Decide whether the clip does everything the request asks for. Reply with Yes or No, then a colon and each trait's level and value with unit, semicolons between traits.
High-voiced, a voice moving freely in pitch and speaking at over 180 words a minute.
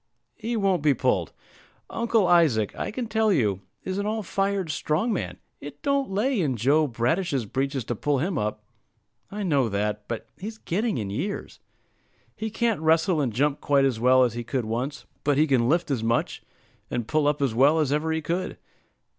No: medium, 150 Hz; wide, 7.5 semitones; average, 195 wpm